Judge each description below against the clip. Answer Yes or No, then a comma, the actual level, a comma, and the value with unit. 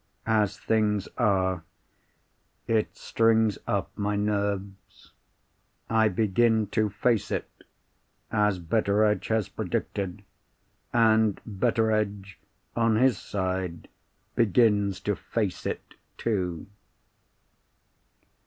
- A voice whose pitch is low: Yes, low, 105 Hz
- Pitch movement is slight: Yes, narrow, 2.2 semitones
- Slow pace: Yes, slow, 90 wpm